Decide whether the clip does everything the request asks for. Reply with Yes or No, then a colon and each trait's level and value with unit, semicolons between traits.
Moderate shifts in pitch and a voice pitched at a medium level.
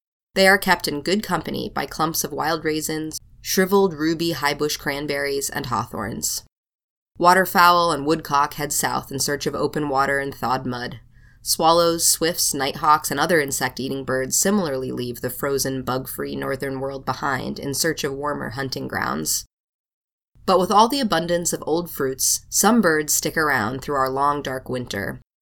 Yes: average, 3.9 semitones; medium, 145 Hz